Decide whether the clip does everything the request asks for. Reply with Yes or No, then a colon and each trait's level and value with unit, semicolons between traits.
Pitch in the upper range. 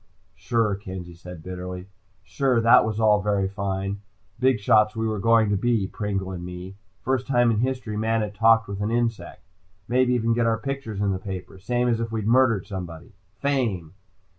No: low, 105 Hz